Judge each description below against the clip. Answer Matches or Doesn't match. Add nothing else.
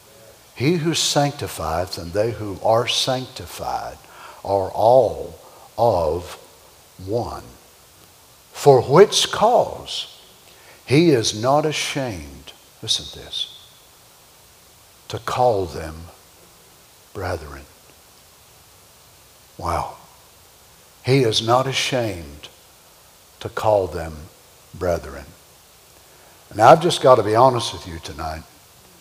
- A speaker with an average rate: Doesn't match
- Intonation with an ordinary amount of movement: Doesn't match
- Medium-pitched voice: Doesn't match